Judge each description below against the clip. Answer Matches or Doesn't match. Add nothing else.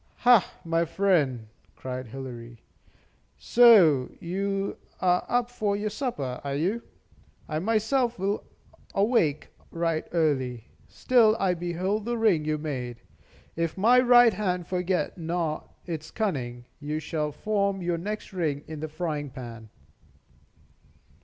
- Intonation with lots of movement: Matches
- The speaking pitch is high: Doesn't match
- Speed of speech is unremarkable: Doesn't match